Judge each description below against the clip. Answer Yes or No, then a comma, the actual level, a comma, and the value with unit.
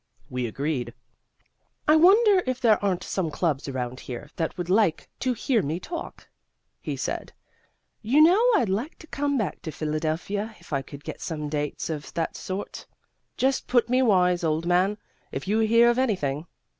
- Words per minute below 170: No, average, 175 wpm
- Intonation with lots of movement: Yes, wide, 7.9 semitones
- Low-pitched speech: No, medium, 185 Hz